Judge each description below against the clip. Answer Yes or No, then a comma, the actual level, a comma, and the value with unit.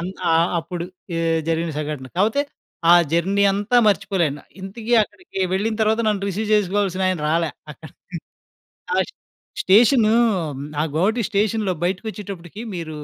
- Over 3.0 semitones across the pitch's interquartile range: Yes, average, 3.9 semitones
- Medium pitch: No, high, 195 Hz